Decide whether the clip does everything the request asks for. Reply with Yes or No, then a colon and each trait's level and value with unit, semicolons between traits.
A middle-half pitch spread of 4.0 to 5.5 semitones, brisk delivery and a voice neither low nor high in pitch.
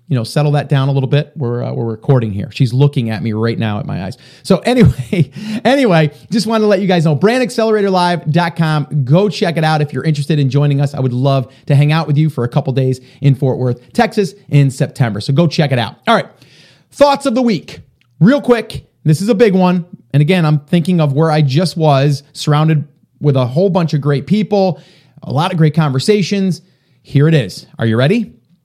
Yes: average, 5.1 semitones; fast, 230 wpm; medium, 155 Hz